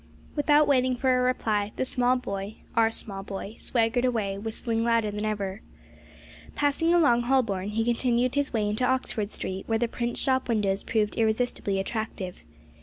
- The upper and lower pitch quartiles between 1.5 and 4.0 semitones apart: Yes, average, 3.4 semitones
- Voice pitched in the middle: No, high, 230 Hz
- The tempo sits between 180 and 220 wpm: No, average, 165 wpm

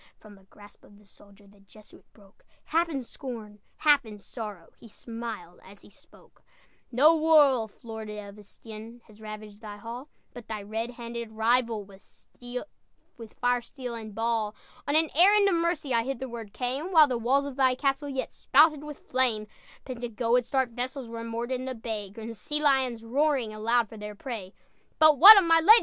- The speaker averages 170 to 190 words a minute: Yes, average, 180 wpm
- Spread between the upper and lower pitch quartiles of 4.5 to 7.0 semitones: No, average, 4.1 semitones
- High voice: Yes, high, 235 Hz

